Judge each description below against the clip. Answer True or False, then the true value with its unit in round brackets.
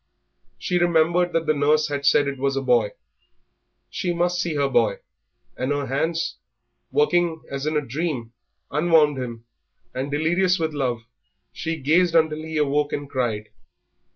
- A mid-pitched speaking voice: True (150 Hz)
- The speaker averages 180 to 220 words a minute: False (155 wpm)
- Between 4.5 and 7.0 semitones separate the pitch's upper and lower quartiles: False (3.2 semitones)